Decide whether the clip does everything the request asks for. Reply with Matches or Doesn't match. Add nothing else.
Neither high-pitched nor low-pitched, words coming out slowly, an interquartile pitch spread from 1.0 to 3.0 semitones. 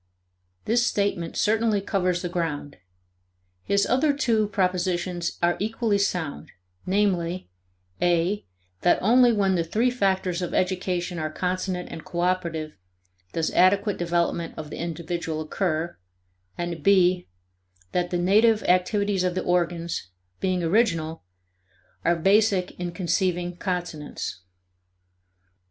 Matches